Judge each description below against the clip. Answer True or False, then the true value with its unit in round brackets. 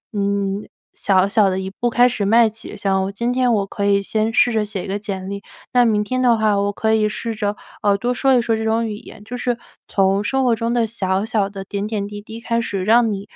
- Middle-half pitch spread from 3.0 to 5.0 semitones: False (2.5 semitones)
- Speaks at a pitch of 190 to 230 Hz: True (210 Hz)